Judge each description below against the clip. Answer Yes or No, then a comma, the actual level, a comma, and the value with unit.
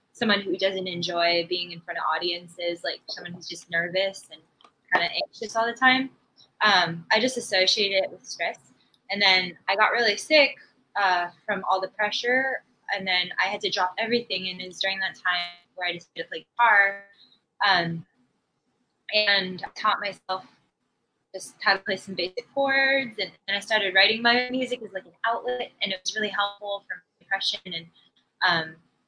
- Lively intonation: No, average, 3.5 semitones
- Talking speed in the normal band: Yes, average, 185 wpm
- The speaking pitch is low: No, high, 195 Hz